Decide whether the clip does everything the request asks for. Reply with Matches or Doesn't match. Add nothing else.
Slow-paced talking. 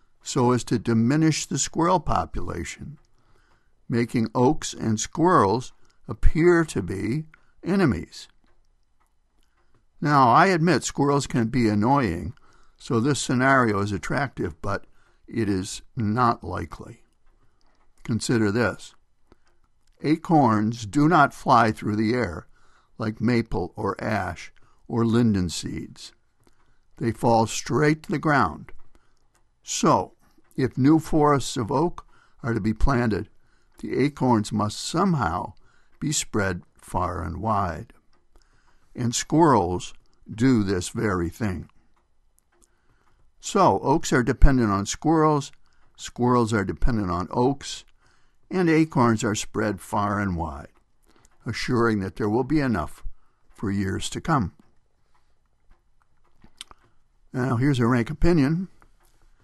Matches